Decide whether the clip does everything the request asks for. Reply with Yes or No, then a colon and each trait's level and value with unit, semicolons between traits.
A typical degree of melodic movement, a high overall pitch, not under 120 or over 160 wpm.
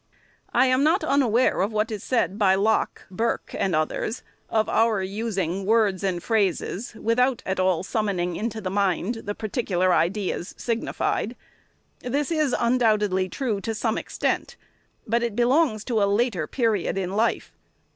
Yes: average, 3.7 semitones; high, 215 Hz; average, 155 wpm